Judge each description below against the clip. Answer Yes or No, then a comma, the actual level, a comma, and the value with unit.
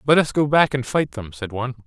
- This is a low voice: Yes, low, 130 Hz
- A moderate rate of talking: No, fast, 290 wpm